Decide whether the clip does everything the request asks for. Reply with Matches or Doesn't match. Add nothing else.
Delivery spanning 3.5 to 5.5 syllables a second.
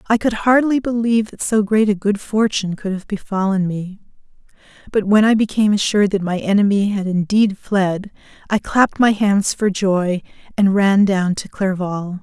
Matches